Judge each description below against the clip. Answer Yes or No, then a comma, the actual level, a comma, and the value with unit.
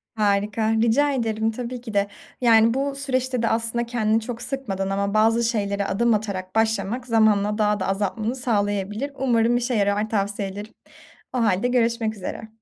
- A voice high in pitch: Yes, high, 220 Hz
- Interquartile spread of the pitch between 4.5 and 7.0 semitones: No, average, 2.7 semitones